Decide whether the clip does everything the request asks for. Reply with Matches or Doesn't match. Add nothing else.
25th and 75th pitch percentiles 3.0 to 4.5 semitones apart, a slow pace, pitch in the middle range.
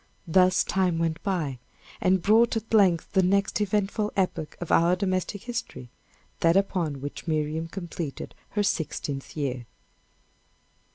Matches